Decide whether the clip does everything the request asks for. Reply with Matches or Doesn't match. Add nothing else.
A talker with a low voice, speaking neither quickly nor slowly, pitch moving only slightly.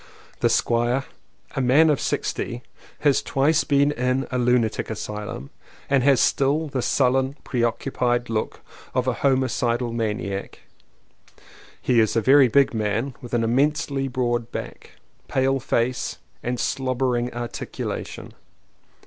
Doesn't match